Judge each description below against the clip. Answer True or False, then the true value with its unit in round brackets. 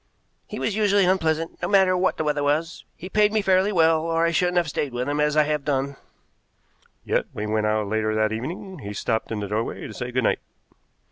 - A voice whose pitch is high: False (150 Hz)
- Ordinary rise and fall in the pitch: False (7.0 semitones)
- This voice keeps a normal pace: False (230 wpm)